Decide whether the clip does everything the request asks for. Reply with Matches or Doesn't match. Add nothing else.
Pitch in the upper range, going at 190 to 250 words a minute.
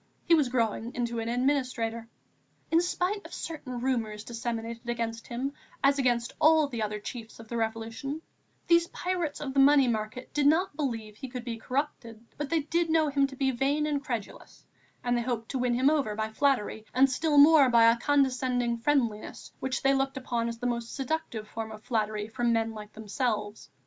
Matches